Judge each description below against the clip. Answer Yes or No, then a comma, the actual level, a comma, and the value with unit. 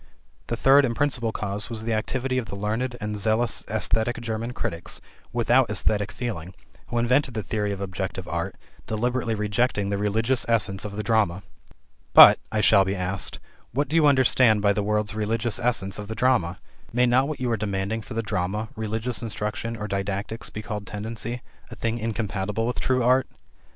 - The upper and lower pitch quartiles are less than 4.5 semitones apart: Yes, average, 2.8 semitones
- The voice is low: Yes, low, 110 Hz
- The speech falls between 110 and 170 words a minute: No, average, 185 wpm